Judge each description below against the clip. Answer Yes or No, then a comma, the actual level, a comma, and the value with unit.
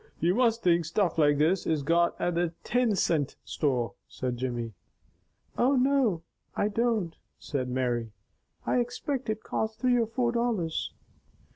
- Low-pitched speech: No, medium, 175 Hz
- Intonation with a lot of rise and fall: Yes, wide, 8.1 semitones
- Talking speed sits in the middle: Yes, average, 150 wpm